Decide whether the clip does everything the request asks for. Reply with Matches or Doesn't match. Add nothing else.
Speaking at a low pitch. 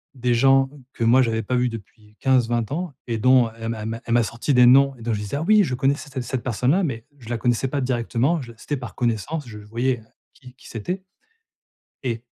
Matches